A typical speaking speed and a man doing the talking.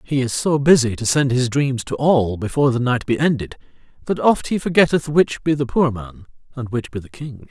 No: fast, 230 wpm; male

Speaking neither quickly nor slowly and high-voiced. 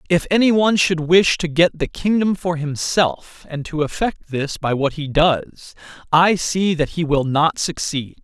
No: average, 190 wpm; medium, 165 Hz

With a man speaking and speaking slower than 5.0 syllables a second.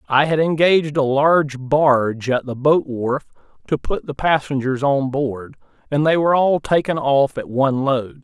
Yes: male; 4.7 syllables/s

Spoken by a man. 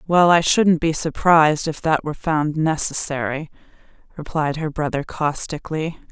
No: female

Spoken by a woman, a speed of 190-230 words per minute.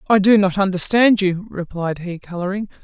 No: female; average, 170 wpm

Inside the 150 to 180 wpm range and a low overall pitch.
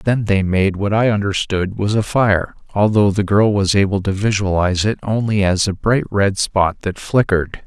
No: average, 195 wpm; low, 100 Hz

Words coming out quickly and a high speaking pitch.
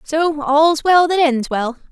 No: average, 190 wpm; very high, 300 Hz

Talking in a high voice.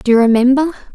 Yes: very high, 255 Hz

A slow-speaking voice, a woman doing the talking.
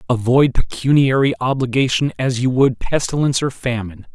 No: slow, 130 wpm; male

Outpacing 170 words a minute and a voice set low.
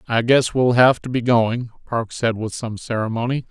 Yes: fast, 205 wpm; low, 120 Hz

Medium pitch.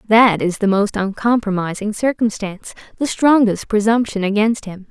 No: high, 210 Hz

